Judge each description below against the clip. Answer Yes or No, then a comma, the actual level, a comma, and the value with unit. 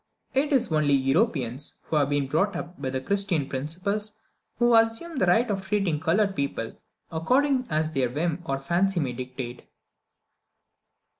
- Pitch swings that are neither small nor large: No, wide, 7.0 semitones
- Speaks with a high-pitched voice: No, medium, 165 Hz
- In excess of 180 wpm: No, average, 150 wpm